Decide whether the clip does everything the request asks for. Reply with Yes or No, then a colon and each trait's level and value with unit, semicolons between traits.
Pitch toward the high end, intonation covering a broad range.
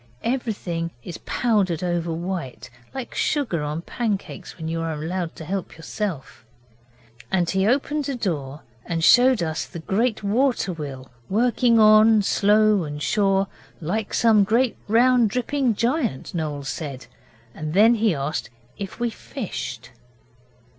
Yes: high, 195 Hz; wide, 6.0 semitones